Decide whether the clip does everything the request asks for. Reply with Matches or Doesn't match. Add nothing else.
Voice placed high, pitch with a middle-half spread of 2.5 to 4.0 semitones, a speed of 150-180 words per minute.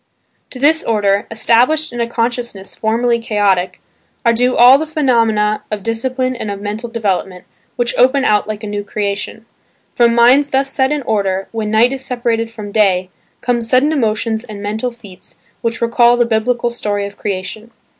Matches